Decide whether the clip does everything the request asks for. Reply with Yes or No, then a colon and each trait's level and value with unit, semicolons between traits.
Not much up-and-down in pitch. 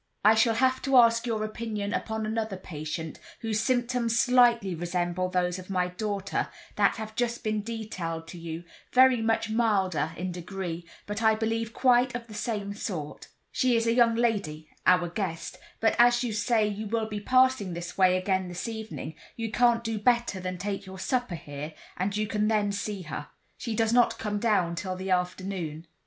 No: average, 4.0 semitones